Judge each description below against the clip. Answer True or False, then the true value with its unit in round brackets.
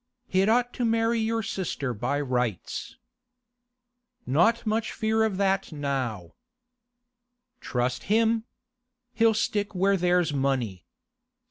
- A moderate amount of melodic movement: False (8.4 semitones)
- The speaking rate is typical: False (110 wpm)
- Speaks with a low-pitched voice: False (195 Hz)